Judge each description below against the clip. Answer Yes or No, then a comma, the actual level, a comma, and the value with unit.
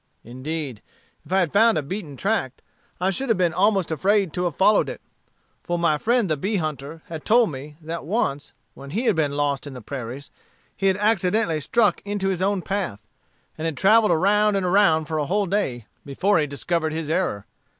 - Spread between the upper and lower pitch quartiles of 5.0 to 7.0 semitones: Yes, wide, 5.4 semitones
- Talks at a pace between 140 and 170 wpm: No, average, 200 wpm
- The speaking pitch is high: No, medium, 175 Hz